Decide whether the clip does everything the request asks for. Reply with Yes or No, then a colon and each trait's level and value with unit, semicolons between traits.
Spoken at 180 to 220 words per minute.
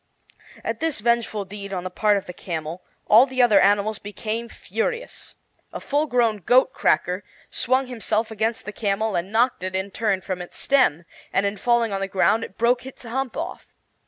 Yes: average, 190 wpm